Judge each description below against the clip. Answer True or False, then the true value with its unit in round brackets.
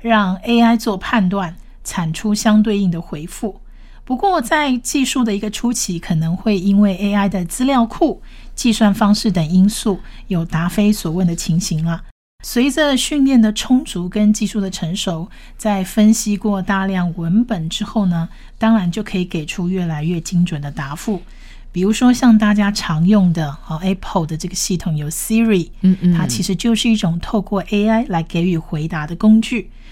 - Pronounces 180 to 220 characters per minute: False (275 characters per minute)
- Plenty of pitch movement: False (3.9 semitones)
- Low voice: False (200 Hz)